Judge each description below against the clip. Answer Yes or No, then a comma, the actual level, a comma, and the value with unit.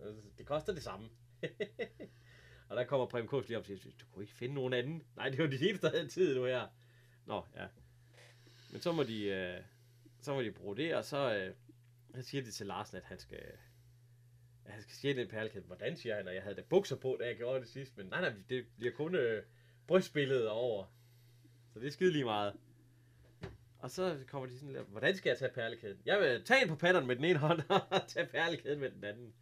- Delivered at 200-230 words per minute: Yes, average, 220 wpm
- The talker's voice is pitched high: No, low, 120 Hz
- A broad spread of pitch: No, average, 3.1 semitones